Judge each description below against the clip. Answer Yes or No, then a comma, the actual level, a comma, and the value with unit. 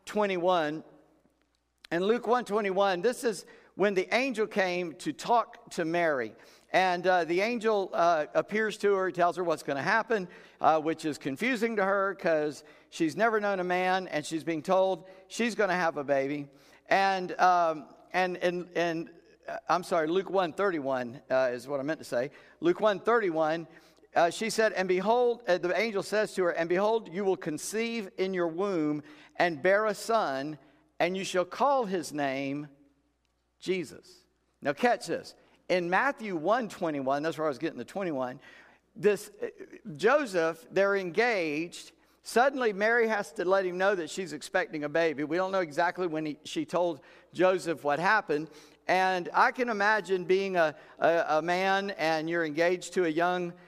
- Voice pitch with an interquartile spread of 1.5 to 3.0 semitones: No, average, 4.0 semitones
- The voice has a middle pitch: Yes, medium, 180 Hz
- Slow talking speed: No, average, 175 wpm